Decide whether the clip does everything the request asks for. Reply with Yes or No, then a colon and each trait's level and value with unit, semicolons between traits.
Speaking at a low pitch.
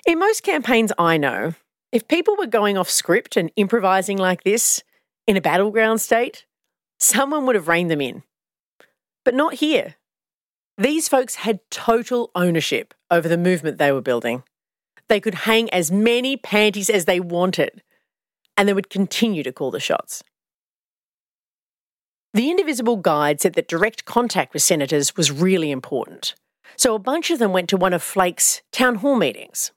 No: high, 205 Hz